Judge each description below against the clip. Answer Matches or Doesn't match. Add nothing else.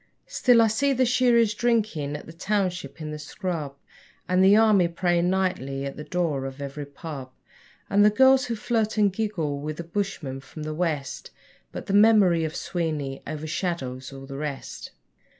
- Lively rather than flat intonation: Matches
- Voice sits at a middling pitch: Matches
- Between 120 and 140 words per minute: Doesn't match